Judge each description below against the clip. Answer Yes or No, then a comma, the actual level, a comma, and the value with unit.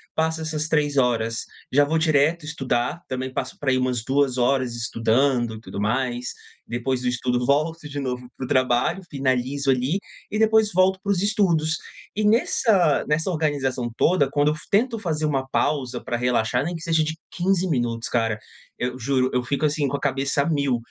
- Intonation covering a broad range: No, average, 4.2 semitones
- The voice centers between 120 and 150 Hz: Yes, medium, 140 Hz